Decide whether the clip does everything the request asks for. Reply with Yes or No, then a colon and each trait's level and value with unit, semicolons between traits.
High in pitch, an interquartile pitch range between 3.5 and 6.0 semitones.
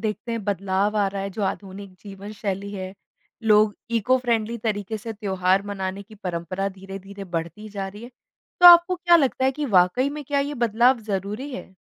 No: high, 205 Hz; average, 3.1 semitones